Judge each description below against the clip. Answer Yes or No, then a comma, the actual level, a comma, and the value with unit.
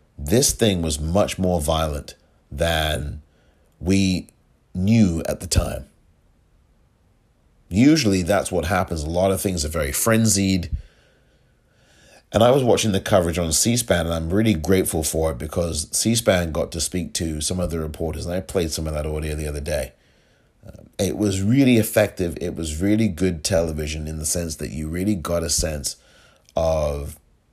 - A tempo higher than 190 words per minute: No, average, 170 wpm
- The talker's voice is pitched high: No, very low, 85 Hz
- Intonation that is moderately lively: Yes, average, 3.7 semitones